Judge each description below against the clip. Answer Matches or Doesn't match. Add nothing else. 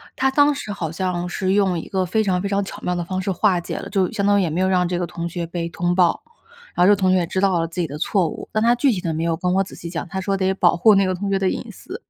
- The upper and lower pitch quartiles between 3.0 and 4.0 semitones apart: Doesn't match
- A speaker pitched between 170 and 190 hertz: Matches